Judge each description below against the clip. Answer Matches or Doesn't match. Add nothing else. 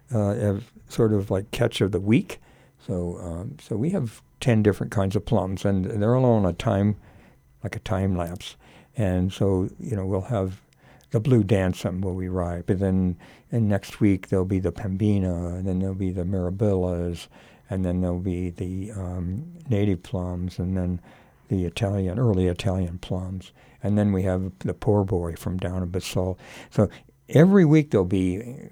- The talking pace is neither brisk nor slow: Matches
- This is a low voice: Matches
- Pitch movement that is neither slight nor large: Matches